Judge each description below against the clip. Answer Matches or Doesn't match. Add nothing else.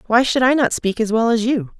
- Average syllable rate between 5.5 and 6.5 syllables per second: Matches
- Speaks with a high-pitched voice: Matches